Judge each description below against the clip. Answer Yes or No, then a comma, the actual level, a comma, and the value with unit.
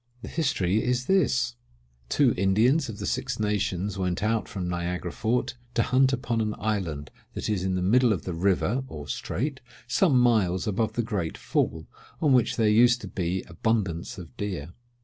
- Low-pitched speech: Yes, low, 105 Hz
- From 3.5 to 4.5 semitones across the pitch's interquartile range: No, average, 5.3 semitones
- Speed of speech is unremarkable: Yes, average, 175 wpm